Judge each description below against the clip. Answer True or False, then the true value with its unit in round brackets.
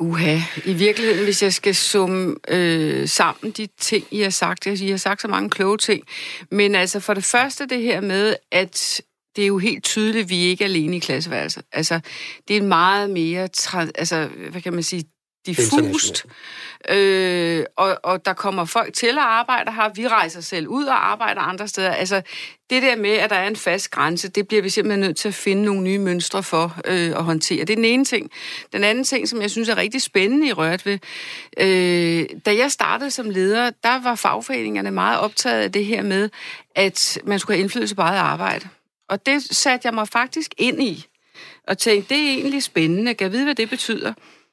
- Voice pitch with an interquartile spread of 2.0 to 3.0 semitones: False (3.8 semitones)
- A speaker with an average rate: True (210 wpm)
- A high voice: True (200 Hz)